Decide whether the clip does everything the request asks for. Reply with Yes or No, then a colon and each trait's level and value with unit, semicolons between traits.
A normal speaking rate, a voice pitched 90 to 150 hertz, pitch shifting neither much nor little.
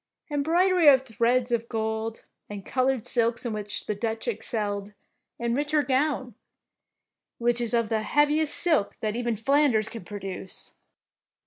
No: average, 155 wpm; high, 235 Hz; average, 3.8 semitones